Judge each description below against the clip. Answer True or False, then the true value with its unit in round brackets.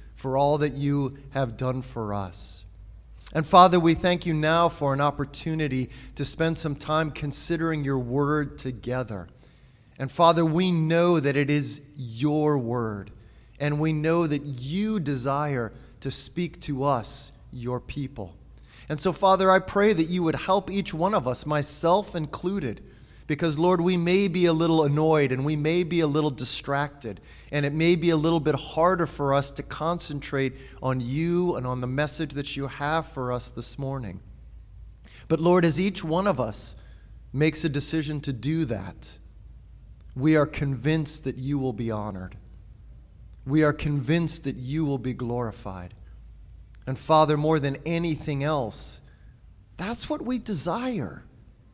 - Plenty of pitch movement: False (4.5 semitones)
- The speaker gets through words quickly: False (160 wpm)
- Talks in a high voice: False (145 Hz)